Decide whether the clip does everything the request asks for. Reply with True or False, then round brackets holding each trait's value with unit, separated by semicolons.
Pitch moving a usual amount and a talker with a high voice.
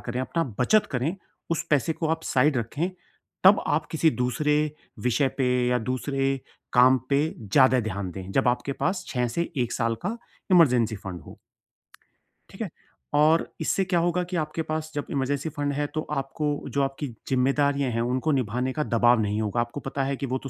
False (3.7 semitones; 135 Hz)